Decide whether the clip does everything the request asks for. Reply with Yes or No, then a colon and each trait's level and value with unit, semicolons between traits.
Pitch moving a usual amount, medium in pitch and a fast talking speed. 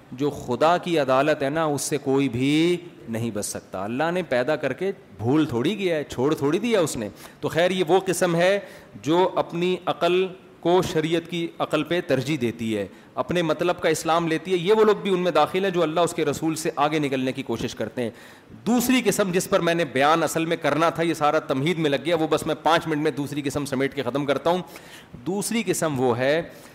Yes: average, 4.2 semitones; medium, 160 Hz; fast, 235 wpm